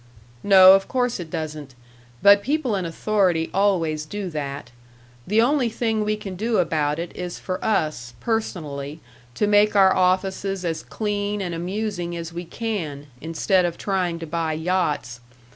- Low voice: No, medium, 185 Hz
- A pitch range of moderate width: Yes, average, 4.2 semitones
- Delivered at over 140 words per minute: Yes, average, 160 wpm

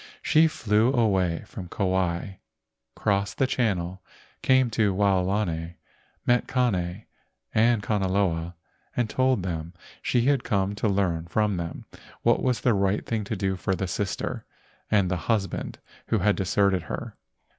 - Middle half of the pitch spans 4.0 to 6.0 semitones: No, average, 3.3 semitones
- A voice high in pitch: No, low, 100 Hz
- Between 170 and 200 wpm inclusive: No, average, 145 wpm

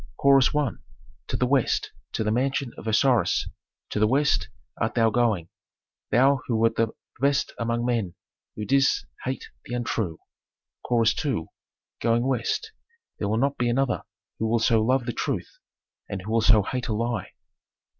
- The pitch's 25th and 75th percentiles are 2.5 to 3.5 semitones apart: Yes, average, 3.0 semitones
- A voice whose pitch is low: Yes, low, 120 Hz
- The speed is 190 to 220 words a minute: No, average, 165 wpm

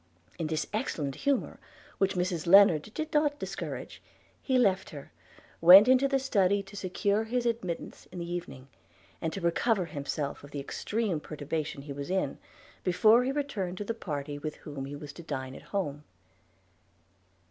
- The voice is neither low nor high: Yes, medium, 180 Hz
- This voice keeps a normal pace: Yes, average, 170 wpm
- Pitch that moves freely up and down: Yes, wide, 6.6 semitones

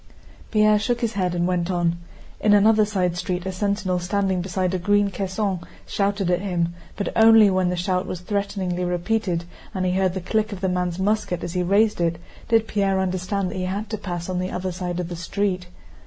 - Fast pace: Yes, fast, 215 wpm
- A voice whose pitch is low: No, medium, 185 Hz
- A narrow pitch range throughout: Yes, narrow, 2.3 semitones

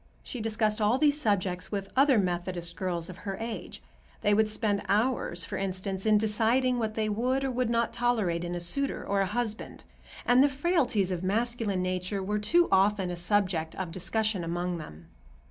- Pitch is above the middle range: Yes, high, 210 Hz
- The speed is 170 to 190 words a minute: Yes, average, 185 wpm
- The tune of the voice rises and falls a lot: No, average, 4.3 semitones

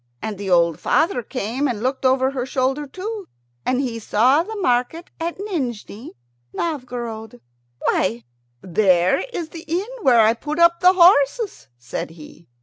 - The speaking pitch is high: Yes, very high, 260 Hz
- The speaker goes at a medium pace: Yes, average, 150 wpm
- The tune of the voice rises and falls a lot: Yes, wide, 7.4 semitones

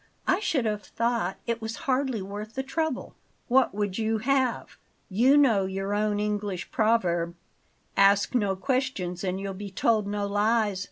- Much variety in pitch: No, average, 3.6 semitones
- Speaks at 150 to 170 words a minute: Yes, average, 160 wpm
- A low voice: No, high, 210 Hz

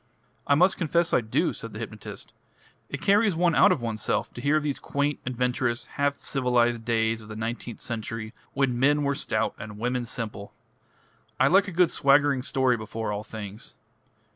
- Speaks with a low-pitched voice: Yes, low, 125 Hz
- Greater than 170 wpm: Yes, average, 180 wpm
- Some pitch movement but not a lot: Yes, average, 4.2 semitones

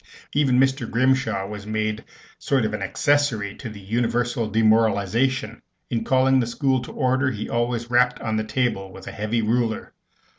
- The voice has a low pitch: Yes, low, 115 Hz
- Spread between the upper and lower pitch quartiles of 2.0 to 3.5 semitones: Yes, average, 3.1 semitones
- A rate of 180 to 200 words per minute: No, average, 170 wpm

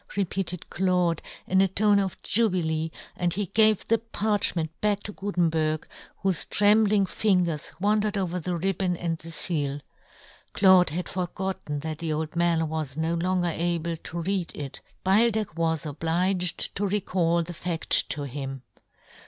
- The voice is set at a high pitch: No, medium, 175 Hz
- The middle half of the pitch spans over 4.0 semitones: No, average, 3.2 semitones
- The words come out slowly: No, average, 155 wpm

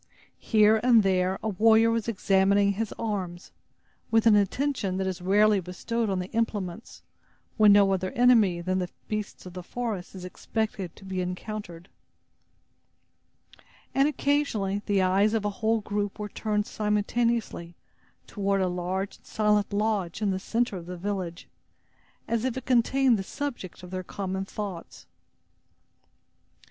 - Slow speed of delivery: No, average, 150 wpm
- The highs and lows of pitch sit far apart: No, average, 3.1 semitones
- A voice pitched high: Yes, high, 205 Hz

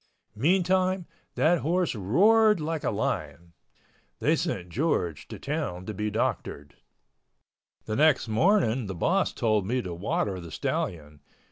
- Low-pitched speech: Yes, low, 120 Hz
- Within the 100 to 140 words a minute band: Yes, slow, 135 wpm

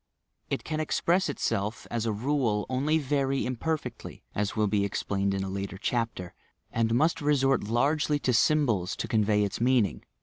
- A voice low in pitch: Yes, low, 120 Hz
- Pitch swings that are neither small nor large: No, wide, 5.7 semitones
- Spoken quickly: No, average, 170 wpm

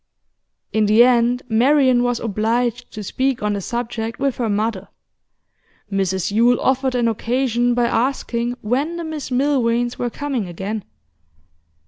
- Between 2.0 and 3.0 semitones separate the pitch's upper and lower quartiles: Yes, narrow, 2.5 semitones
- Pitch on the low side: No, high, 240 Hz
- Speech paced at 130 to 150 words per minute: Yes, average, 140 wpm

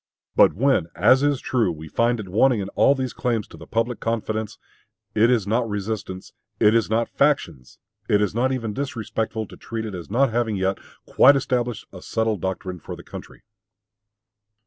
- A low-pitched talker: Yes, low, 110 Hz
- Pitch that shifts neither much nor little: Yes, average, 3.2 semitones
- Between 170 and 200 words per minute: Yes, average, 185 wpm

